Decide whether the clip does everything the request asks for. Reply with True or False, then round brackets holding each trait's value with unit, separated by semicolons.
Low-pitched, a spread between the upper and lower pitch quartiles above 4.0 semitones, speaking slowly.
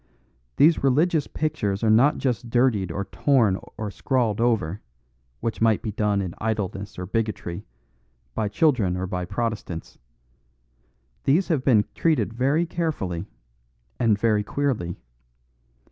True (110 Hz; 5.2 semitones; 130 wpm)